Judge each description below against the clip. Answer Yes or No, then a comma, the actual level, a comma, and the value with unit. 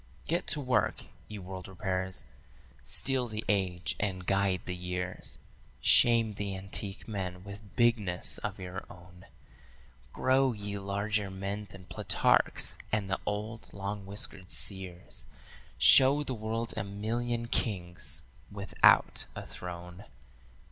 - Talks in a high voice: No, low, 100 Hz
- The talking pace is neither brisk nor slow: No, slow, 125 wpm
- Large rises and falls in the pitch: No, average, 2.9 semitones